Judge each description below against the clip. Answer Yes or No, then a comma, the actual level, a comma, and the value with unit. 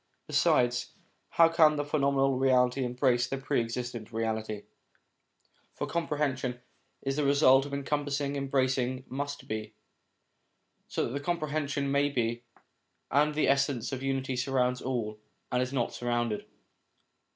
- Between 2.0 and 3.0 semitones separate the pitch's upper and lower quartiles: Yes, narrow, 2.6 semitones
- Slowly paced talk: Yes, slow, 130 wpm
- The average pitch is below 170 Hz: Yes, low, 135 Hz